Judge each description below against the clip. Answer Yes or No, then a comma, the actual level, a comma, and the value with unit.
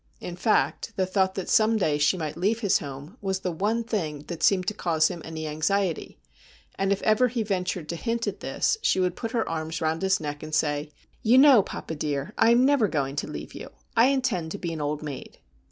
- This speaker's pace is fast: Yes, fast, 235 wpm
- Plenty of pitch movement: Yes, wide, 5.7 semitones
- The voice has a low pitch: No, medium, 185 Hz